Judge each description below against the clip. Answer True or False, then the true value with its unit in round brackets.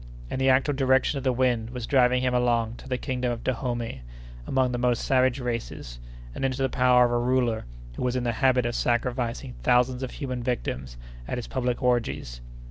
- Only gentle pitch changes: True (1.5 semitones)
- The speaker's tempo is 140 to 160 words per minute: False (205 wpm)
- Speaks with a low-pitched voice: True (125 Hz)